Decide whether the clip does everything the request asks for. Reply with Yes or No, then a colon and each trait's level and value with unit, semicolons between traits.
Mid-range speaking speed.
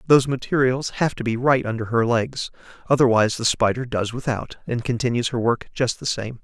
Yes: average, 195 wpm